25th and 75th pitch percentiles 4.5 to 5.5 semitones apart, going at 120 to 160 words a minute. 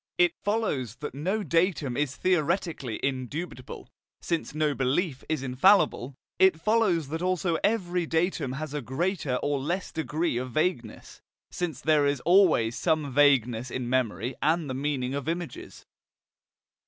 Yes: average, 5.1 semitones; average, 140 wpm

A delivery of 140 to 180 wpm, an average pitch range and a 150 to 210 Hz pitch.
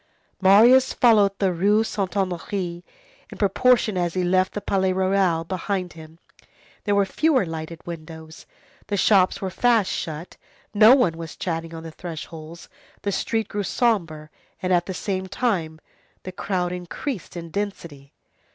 Yes: average, 150 wpm; average, 3.5 semitones; medium, 185 Hz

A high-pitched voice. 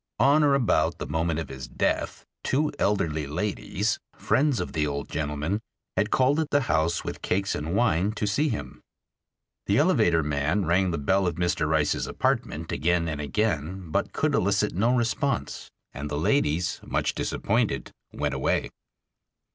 No: very low, 85 Hz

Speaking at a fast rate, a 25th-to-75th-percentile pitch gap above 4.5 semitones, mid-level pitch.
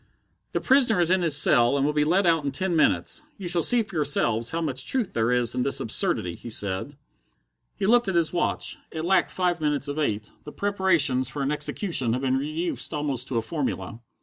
Yes: fast, 220 wpm; average, 5.2 semitones; medium, 150 Hz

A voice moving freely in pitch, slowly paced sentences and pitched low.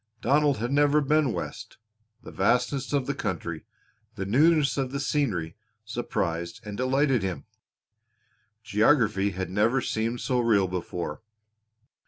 Yes: wide, 6.3 semitones; slow, 130 wpm; low, 120 Hz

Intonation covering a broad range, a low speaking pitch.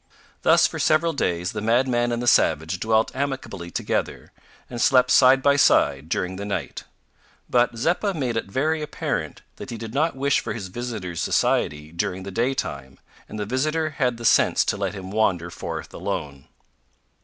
Yes: wide, 6.1 semitones; low, 115 Hz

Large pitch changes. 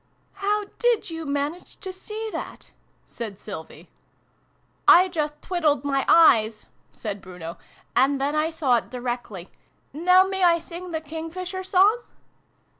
Yes: wide, 6.4 semitones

